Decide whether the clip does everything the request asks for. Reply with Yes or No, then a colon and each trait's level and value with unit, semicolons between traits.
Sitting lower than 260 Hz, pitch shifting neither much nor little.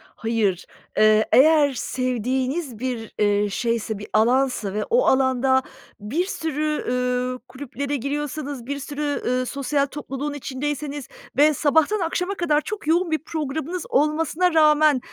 No: very high, 280 Hz; average, 3.4 semitones